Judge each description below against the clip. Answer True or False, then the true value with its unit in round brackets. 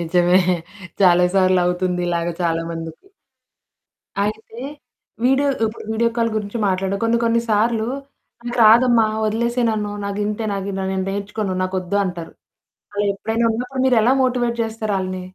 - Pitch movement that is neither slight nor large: True (3.7 semitones)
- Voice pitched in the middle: False (210 Hz)